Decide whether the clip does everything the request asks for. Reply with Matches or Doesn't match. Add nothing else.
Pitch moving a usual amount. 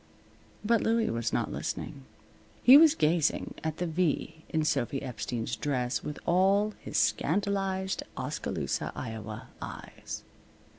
Doesn't match